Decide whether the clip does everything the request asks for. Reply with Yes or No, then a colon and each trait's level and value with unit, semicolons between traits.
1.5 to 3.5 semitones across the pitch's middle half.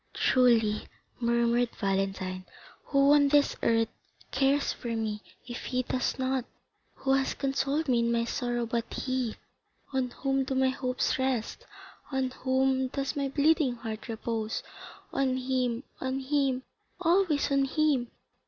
Yes: narrow, 2.6 semitones